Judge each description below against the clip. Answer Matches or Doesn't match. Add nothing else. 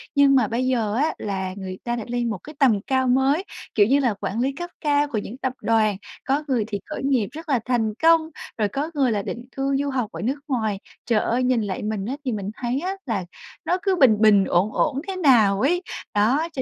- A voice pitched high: Matches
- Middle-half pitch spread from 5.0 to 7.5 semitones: Doesn't match